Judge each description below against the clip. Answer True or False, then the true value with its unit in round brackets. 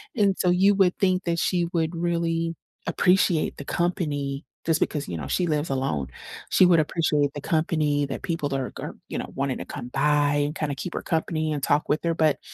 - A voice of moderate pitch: True (155 Hz)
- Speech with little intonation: False (3.0 semitones)